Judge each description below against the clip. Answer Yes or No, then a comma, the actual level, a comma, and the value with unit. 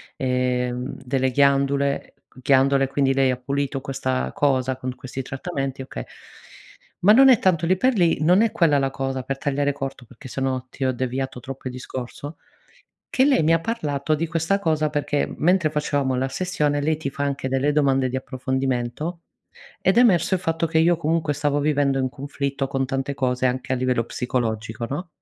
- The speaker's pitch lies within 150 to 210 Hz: No, medium, 140 Hz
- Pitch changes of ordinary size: Yes, average, 3.0 semitones